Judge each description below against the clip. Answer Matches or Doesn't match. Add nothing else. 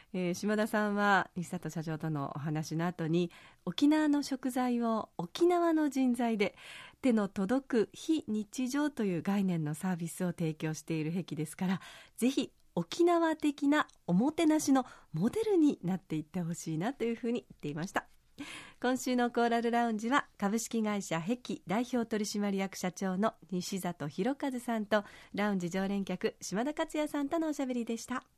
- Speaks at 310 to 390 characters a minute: Matches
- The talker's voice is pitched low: Doesn't match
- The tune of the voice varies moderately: Doesn't match